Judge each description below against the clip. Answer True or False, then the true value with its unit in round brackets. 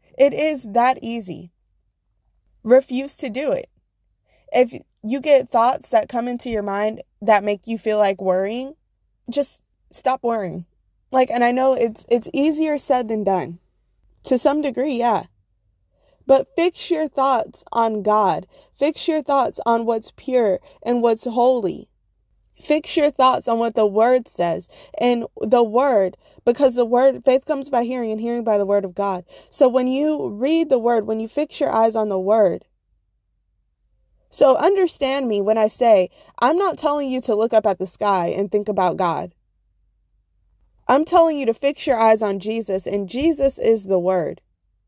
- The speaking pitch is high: True (235 Hz)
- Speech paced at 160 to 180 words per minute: True (170 wpm)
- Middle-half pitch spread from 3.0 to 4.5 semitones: False (5.0 semitones)